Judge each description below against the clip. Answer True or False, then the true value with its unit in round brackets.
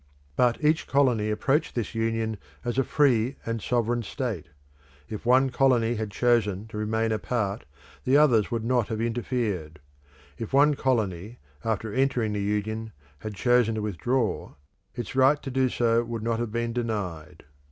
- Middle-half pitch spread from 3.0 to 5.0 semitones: False (2.6 semitones)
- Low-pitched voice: True (115 Hz)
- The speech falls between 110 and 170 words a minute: True (160 wpm)